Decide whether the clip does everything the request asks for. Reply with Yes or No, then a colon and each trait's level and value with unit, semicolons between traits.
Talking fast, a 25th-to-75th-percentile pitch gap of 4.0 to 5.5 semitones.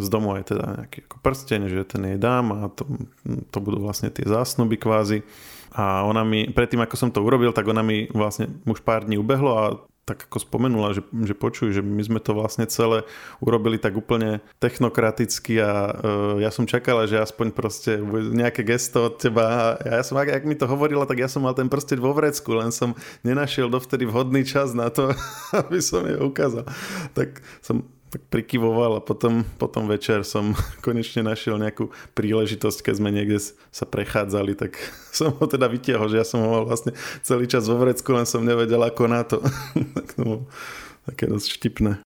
No: fast, 195 wpm; average, 2.8 semitones